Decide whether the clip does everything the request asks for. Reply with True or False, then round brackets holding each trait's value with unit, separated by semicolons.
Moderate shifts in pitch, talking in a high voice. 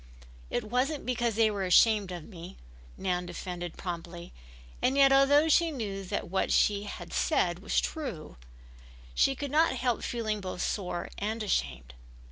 False (6.1 semitones; 210 Hz)